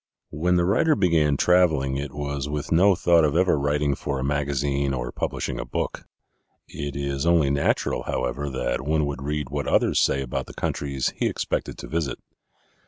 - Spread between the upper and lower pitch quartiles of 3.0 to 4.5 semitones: No, narrow, 2.6 semitones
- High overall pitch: No, very low, 70 Hz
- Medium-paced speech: Yes, average, 180 wpm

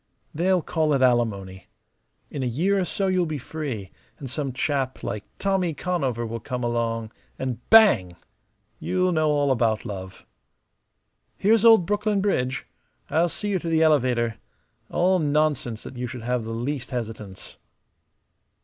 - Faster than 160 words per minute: No, average, 150 wpm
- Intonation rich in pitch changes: Yes, wide, 6.8 semitones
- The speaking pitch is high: No, low, 135 Hz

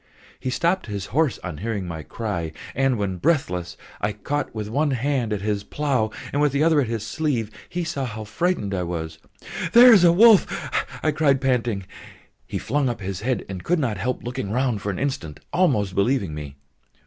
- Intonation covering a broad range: Yes, wide, 6.5 semitones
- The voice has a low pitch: Yes, low, 115 Hz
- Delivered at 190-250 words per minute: Yes, average, 195 wpm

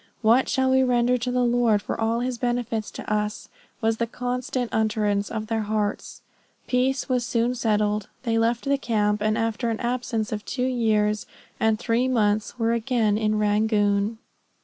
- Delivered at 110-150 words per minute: No, average, 170 wpm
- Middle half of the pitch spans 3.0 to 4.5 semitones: No, narrow, 2.5 semitones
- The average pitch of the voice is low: No, high, 225 Hz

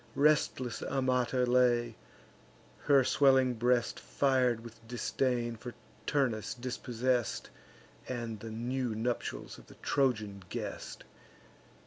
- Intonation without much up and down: Yes, narrow, 1.8 semitones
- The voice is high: No, low, 125 Hz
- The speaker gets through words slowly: Yes, slow, 100 wpm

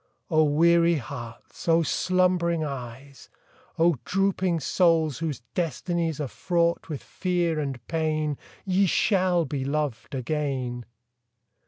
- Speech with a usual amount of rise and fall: Yes, average, 3.6 semitones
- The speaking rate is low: Yes, slow, 115 wpm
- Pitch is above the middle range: No, medium, 160 Hz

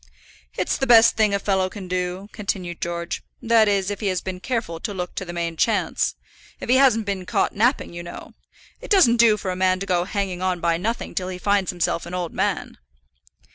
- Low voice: No, high, 190 Hz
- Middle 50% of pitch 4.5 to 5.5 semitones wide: No, average, 3.1 semitones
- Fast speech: Yes, fast, 220 wpm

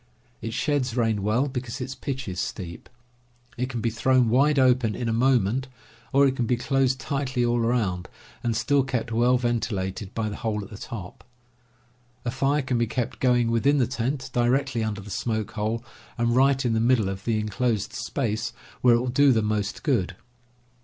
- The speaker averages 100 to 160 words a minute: No, average, 195 wpm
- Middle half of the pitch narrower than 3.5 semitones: Yes, average, 2.8 semitones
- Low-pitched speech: Yes, low, 120 Hz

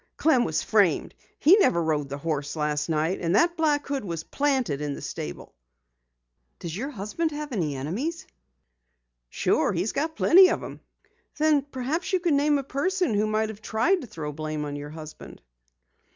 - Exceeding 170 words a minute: Yes, average, 180 wpm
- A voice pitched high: Yes, high, 220 Hz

